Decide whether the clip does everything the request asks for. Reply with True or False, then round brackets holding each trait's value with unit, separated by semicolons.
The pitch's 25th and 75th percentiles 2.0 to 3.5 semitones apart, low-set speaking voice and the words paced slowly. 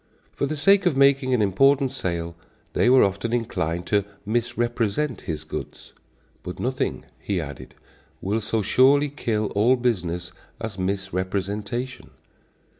False (5.5 semitones; 110 Hz; 130 wpm)